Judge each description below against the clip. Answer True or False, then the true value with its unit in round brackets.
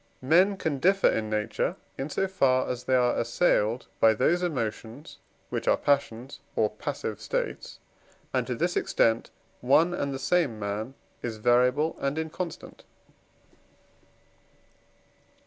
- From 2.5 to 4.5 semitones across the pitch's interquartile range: False (5.6 semitones)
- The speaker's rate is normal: False (130 wpm)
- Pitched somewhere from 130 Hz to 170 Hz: True (135 Hz)